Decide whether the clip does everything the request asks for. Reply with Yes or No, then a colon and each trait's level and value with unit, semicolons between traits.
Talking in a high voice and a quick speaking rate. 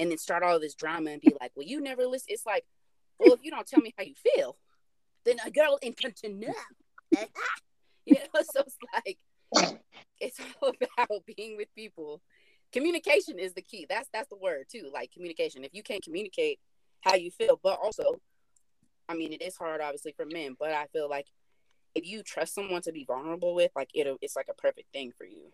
Yes: high, 210 Hz; fast, 215 wpm